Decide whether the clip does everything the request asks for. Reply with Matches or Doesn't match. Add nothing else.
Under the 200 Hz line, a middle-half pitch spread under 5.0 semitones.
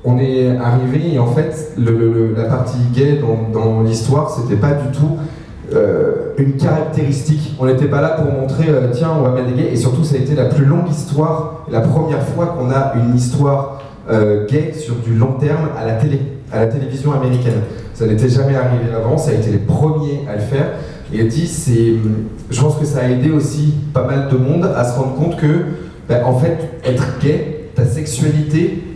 Matches